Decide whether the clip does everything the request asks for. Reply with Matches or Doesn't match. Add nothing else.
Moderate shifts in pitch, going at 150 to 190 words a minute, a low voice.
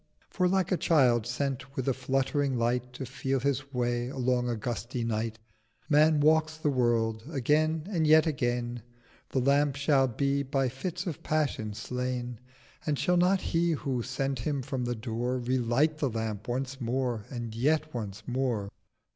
Matches